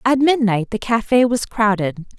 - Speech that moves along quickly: No, average, 165 wpm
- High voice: Yes, high, 225 Hz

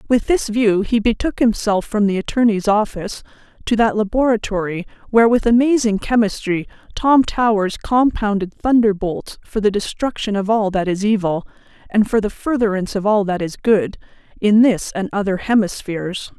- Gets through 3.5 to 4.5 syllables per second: No, 5.1 syllables/s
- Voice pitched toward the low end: No, high, 210 Hz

